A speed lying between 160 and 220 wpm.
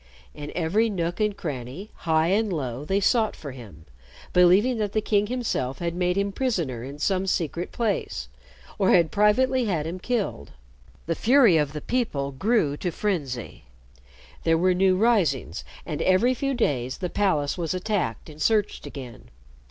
Yes: average, 165 wpm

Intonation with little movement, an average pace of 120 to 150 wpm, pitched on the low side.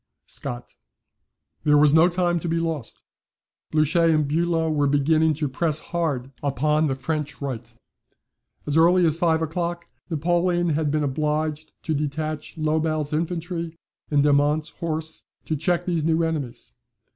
No: narrow, 2.1 semitones; average, 145 wpm; medium, 155 Hz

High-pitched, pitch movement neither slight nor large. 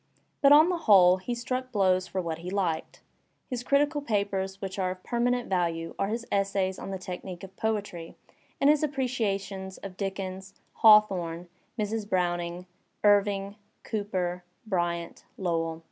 Yes: high, 195 Hz; average, 3.4 semitones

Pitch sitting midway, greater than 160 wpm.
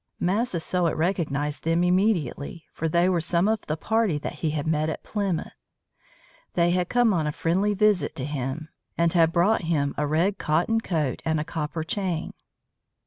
Yes: medium, 170 Hz; average, 175 wpm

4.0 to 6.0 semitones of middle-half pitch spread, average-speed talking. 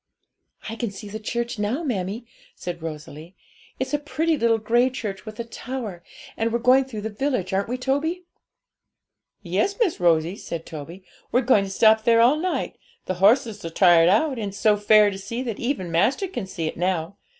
Yes: average, 5.1 semitones; average, 195 wpm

